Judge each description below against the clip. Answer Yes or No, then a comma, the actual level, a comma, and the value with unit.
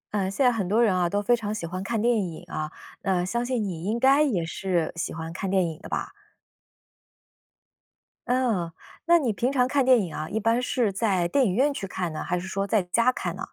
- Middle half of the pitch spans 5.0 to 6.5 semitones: Yes, average, 5.3 semitones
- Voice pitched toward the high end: Yes, high, 205 Hz